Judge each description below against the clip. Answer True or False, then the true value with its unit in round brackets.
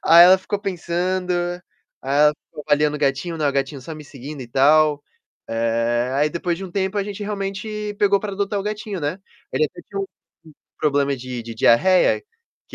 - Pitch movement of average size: False (5.8 semitones)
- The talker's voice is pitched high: False (165 Hz)